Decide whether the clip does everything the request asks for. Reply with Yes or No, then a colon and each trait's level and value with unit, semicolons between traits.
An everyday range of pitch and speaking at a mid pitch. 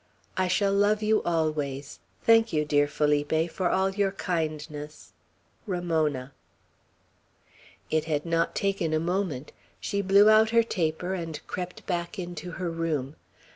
Yes: average, 4.0 semitones; medium, 170 Hz